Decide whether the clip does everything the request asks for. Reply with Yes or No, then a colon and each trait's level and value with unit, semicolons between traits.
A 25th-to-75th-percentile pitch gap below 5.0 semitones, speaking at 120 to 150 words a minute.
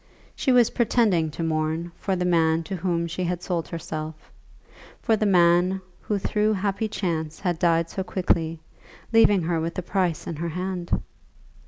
No: narrow, 2.6 semitones; average, 170 wpm